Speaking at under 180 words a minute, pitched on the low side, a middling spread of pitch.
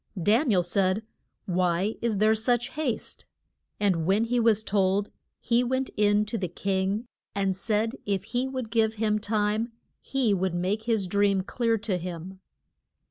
No: average, 165 wpm; high, 210 Hz; average, 3.1 semitones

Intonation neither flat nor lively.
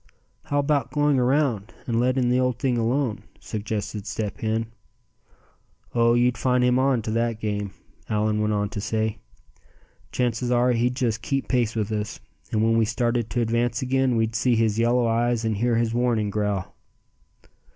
No: narrow, 2.2 semitones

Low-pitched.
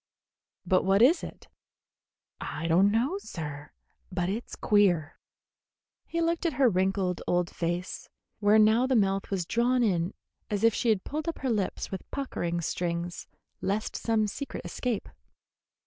No: high, 200 Hz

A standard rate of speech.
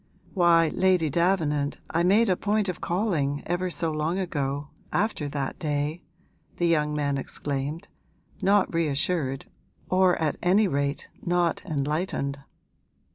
No: slow, 130 wpm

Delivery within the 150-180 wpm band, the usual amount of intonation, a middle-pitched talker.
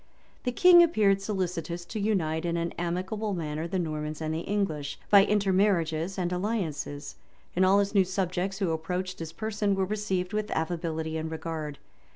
Yes: average, 170 wpm; average, 3.8 semitones; medium, 180 Hz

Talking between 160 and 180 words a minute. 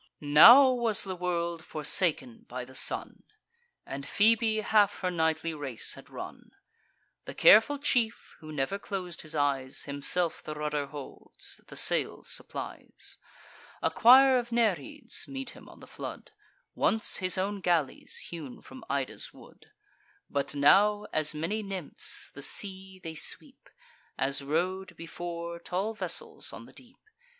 No: average, 140 wpm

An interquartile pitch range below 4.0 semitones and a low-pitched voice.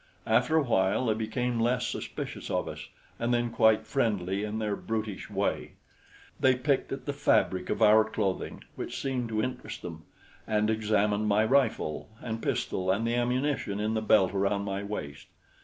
Yes: average, 3.2 semitones; low, 110 Hz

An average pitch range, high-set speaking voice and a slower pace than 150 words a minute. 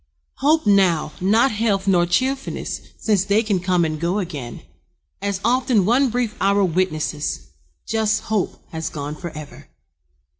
Yes: average, 4.4 semitones; high, 195 Hz; average, 140 wpm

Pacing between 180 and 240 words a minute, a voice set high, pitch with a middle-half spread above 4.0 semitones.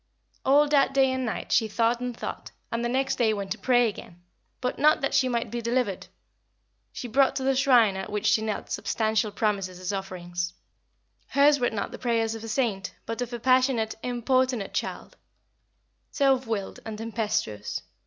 No: average, 185 wpm; high, 230 Hz; average, 3.5 semitones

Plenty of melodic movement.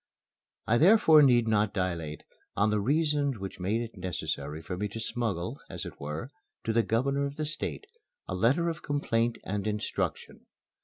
Yes: wide, 6.8 semitones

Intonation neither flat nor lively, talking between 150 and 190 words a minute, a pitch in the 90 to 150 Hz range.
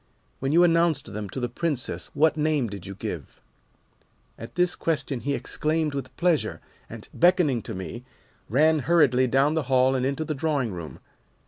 Yes: average, 4.5 semitones; average, 175 wpm; medium, 140 Hz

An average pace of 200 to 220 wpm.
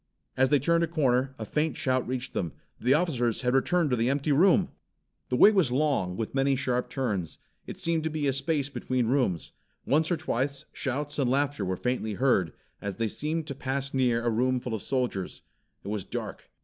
Yes: fast, 205 wpm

